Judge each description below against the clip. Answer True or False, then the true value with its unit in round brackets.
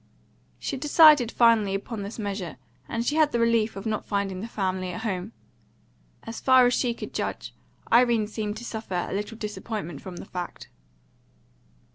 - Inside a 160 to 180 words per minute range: True (170 wpm)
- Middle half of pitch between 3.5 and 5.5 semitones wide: False (3.1 semitones)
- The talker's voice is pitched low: False (220 Hz)